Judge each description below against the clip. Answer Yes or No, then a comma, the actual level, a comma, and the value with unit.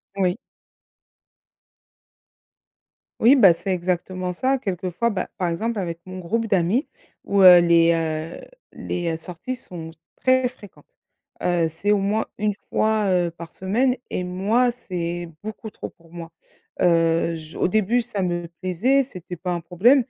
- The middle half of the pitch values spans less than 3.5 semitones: No, average, 4.3 semitones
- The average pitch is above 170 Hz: Yes, medium, 185 Hz